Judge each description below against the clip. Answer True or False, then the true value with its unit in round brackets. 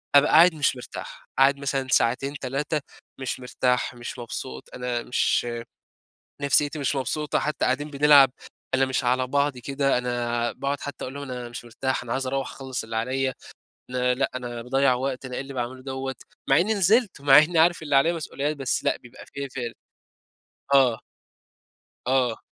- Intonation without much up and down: True (2.2 semitones)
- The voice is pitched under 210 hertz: True (135 Hz)